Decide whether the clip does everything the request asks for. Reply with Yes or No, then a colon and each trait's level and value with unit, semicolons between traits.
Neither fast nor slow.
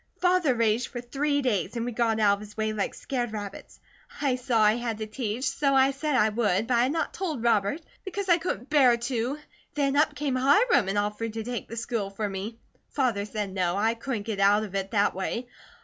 No: fast, 225 wpm